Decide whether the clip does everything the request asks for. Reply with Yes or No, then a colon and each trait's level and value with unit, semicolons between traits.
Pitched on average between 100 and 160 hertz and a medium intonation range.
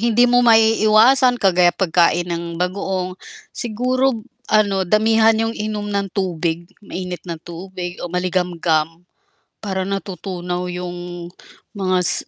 No: high, 190 Hz; average, 3.6 semitones